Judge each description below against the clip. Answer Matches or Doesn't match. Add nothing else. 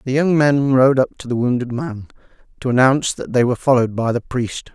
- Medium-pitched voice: Doesn't match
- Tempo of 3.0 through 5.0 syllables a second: Doesn't match